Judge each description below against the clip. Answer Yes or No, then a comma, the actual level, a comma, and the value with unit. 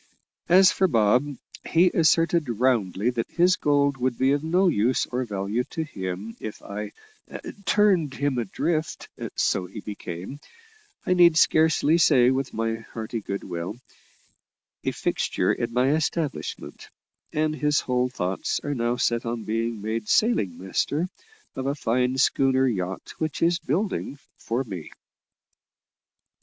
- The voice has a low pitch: Yes, low, 125 Hz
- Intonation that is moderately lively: No, wide, 5.8 semitones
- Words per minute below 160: Yes, average, 140 wpm